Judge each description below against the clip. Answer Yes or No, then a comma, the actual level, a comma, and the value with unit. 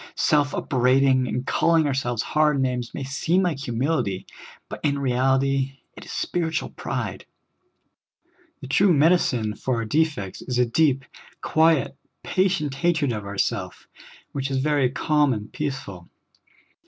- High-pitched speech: No, low, 135 Hz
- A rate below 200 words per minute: Yes, average, 140 wpm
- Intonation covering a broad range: No, average, 3.5 semitones